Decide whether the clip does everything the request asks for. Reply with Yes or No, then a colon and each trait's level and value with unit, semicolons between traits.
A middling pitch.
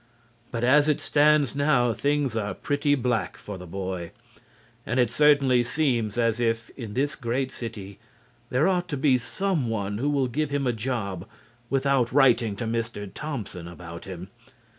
No: low, 120 Hz